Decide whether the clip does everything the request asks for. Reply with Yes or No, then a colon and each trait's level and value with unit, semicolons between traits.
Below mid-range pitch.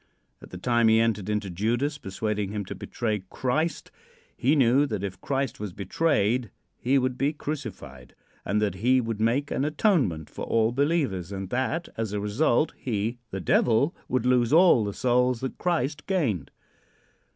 Yes: low, 120 Hz